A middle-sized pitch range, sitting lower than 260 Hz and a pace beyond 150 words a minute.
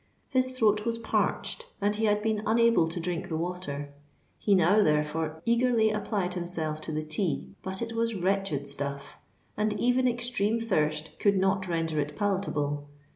No: wide, 5.8 semitones; high, 190 Hz; average, 165 wpm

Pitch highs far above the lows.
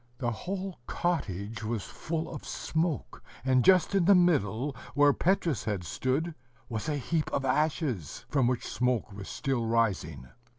Yes: wide, 6.5 semitones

